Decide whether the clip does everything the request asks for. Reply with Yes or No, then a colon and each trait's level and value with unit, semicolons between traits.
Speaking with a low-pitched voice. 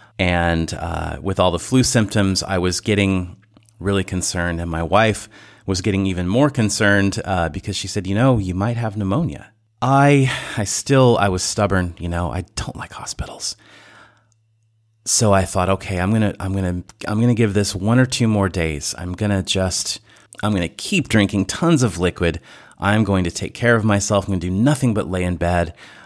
Yes: low, 100 Hz